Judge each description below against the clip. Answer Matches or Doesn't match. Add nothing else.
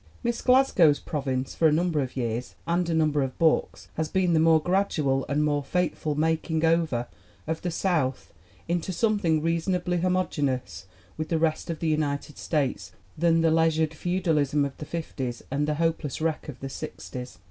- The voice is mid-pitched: Matches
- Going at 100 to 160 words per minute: Doesn't match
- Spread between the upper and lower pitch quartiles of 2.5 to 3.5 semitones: Matches